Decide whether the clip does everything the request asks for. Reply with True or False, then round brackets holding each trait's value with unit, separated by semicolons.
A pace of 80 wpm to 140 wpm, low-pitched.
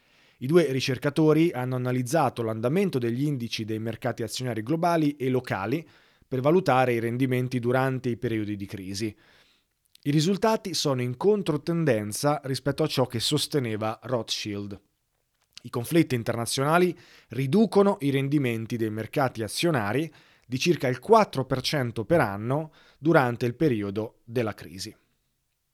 True (125 wpm; 130 Hz)